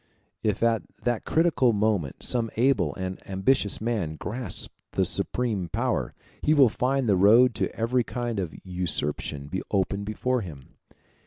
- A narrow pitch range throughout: No, average, 4.7 semitones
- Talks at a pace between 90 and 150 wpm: Yes, average, 145 wpm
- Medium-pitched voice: No, low, 110 Hz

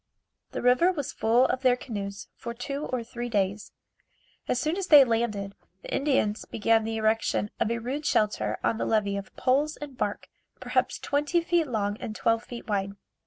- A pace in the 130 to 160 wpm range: No, average, 185 wpm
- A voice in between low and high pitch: No, high, 235 Hz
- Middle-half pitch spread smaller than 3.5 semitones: No, average, 4.6 semitones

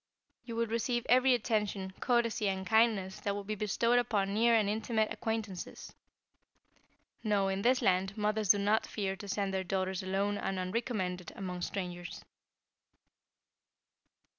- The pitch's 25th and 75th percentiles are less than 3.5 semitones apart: Yes, average, 2.9 semitones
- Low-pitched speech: No, high, 205 Hz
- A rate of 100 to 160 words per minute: Yes, average, 140 wpm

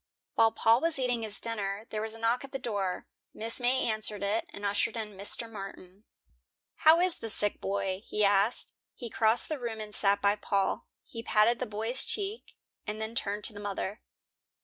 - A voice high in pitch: Yes, high, 220 Hz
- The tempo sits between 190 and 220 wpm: Yes, average, 195 wpm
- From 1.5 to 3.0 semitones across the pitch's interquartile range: Yes, narrow, 2.4 semitones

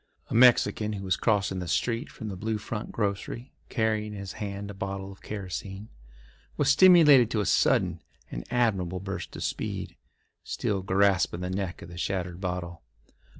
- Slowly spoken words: No, average, 170 wpm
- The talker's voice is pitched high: No, low, 100 Hz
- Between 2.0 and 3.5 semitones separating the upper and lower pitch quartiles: Yes, average, 2.9 semitones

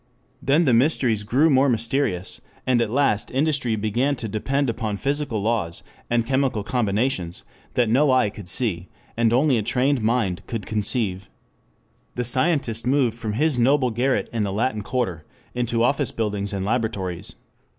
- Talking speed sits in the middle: Yes, average, 160 wpm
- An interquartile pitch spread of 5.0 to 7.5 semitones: No, average, 3.8 semitones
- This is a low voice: Yes, low, 120 Hz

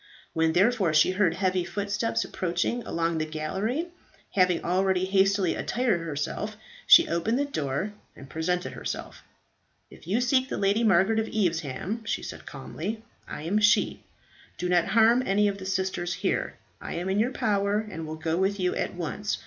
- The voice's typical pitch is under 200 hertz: Yes, high, 190 Hz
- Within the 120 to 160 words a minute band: No, average, 175 wpm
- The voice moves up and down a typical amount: Yes, average, 3.9 semitones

